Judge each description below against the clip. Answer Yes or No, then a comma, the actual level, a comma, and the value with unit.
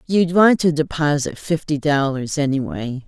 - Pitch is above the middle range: No, medium, 150 Hz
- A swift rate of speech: No, average, 155 wpm